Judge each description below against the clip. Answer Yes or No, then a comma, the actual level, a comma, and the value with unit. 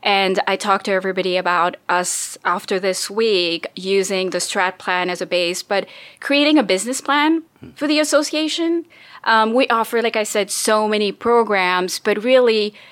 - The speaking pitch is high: Yes, high, 205 Hz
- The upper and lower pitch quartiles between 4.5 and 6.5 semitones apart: Yes, average, 5.0 semitones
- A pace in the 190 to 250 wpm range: No, average, 165 wpm